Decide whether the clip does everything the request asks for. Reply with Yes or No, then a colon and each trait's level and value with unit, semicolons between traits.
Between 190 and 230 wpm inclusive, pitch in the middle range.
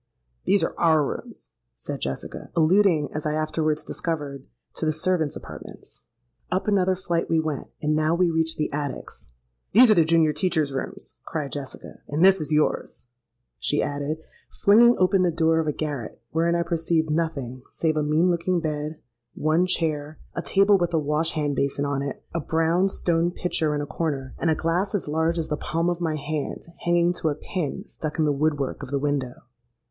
Yes: average, 195 wpm; medium, 160 Hz